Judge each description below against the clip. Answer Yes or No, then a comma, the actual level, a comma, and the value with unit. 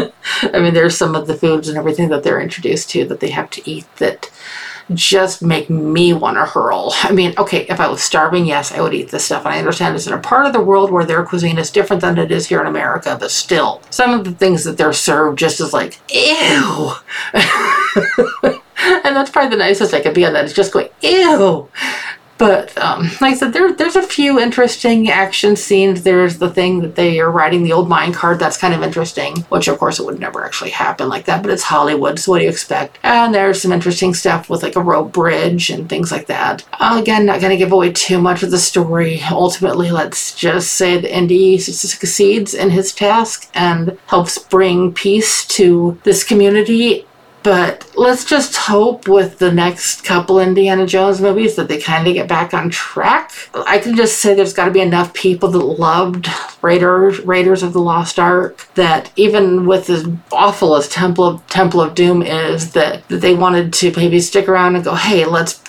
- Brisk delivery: Yes, fast, 210 wpm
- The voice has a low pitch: No, medium, 185 Hz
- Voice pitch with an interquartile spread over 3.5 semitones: No, narrow, 2.6 semitones